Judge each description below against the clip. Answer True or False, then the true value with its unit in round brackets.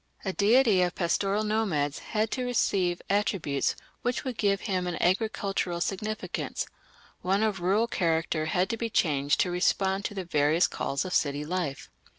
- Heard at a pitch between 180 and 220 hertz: True (190 Hz)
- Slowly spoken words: False (160 wpm)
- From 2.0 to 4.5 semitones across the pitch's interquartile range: True (3.7 semitones)